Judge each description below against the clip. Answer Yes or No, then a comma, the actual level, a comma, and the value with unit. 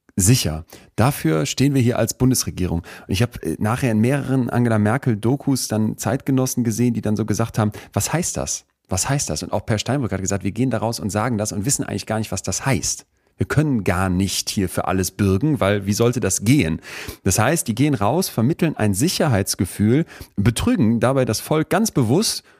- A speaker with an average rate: No, fast, 200 wpm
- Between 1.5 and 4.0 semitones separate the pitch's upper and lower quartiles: No, average, 4.7 semitones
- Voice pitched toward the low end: Yes, low, 110 Hz